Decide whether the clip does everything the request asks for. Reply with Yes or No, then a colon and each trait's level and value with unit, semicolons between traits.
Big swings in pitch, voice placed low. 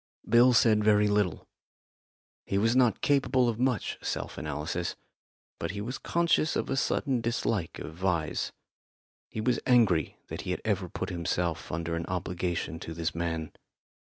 Yes: wide, 6.1 semitones; low, 100 Hz